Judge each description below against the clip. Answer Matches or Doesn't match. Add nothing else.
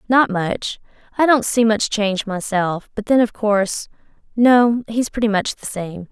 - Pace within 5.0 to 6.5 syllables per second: Doesn't match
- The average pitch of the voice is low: Doesn't match